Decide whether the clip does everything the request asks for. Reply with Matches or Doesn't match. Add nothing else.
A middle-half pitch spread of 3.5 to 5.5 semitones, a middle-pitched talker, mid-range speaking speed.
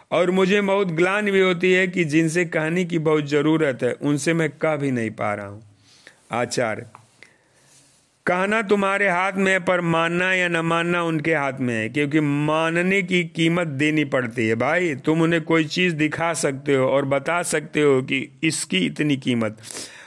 Matches